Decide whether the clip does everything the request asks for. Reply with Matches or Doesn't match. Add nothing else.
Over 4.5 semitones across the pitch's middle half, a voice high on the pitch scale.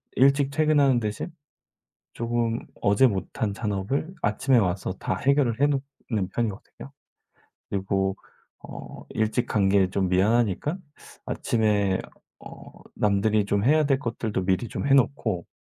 Doesn't match